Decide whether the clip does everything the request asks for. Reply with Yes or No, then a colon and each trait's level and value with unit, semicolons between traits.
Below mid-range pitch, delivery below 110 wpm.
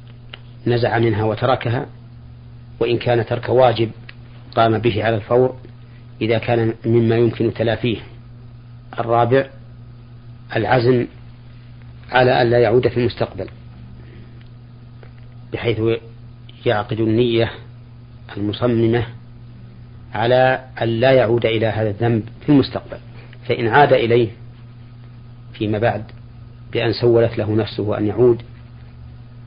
Yes: low, 120 Hz; average, 95 wpm